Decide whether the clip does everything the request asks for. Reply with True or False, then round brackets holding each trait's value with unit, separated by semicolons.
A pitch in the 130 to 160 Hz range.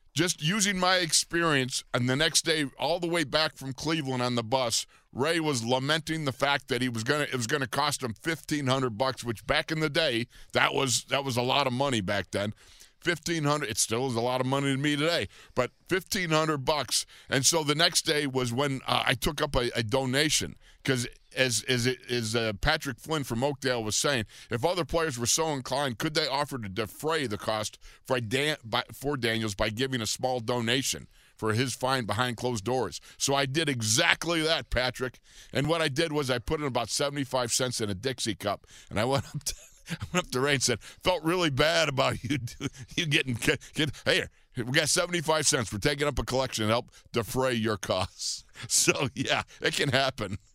True (135 Hz)